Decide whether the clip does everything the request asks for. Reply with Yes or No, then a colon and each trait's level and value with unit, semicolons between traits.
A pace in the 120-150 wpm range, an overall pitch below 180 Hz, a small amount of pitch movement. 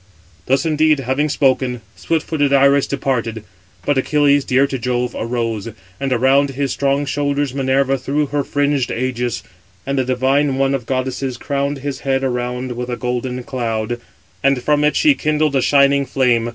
No: average, 165 wpm; low, 135 Hz; narrow, 2.2 semitones